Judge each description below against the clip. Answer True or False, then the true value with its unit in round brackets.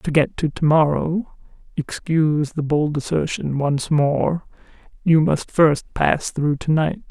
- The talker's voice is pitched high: False (155 Hz)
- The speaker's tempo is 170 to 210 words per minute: False (150 wpm)